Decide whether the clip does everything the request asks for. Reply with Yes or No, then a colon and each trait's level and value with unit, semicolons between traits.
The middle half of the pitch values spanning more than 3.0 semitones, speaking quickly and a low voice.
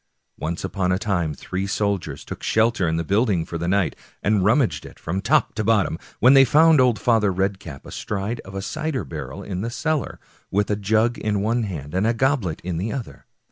Yes: average, 3.9 semitones; fast, 215 wpm; low, 100 Hz